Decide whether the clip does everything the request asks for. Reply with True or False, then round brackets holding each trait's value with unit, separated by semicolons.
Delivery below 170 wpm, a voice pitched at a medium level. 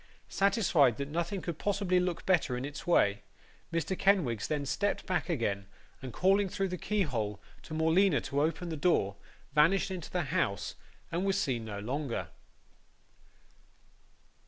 True (150 wpm; 160 Hz)